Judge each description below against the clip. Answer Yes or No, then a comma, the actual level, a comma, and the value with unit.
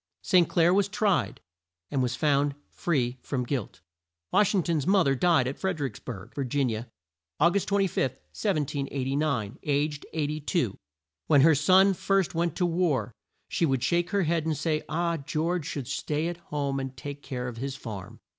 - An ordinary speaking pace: Yes, average, 185 wpm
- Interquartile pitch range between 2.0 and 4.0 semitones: No, average, 4.4 semitones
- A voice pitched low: No, medium, 150 Hz